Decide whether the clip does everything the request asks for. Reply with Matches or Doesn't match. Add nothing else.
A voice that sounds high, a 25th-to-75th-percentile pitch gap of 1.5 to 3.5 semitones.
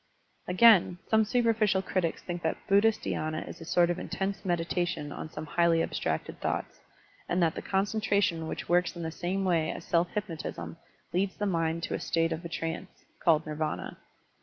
Doesn't match